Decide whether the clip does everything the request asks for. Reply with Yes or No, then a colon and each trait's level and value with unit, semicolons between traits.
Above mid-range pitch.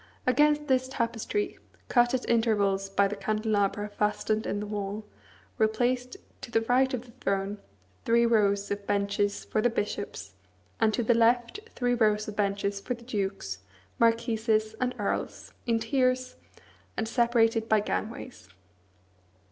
Yes: high, 220 Hz